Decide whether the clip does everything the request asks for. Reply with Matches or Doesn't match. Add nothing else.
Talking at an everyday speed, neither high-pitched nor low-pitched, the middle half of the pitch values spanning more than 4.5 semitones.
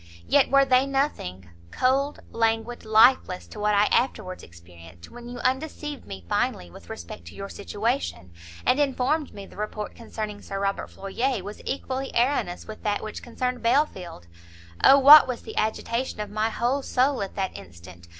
Doesn't match